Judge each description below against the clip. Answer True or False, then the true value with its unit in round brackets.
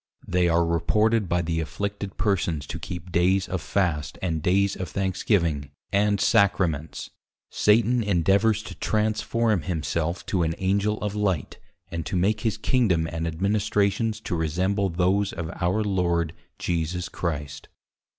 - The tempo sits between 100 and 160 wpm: True (140 wpm)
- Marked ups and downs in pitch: False (3.4 semitones)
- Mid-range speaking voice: False (95 Hz)